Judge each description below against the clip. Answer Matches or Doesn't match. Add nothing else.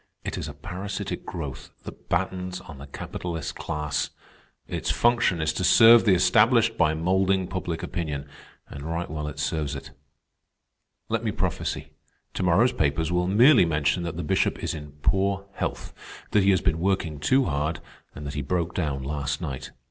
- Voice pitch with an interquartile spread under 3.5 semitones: Doesn't match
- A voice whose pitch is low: Matches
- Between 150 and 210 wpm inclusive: Matches